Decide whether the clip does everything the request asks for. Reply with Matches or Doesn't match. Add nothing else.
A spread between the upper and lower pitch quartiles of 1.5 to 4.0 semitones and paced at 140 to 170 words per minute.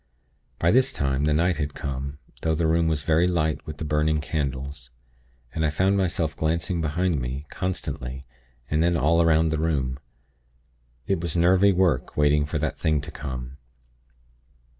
Matches